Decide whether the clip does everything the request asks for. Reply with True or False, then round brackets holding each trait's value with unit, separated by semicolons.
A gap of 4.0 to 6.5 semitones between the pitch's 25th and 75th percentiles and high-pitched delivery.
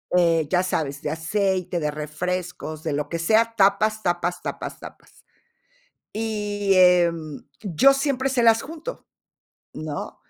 False (5.1 semitones; 180 Hz)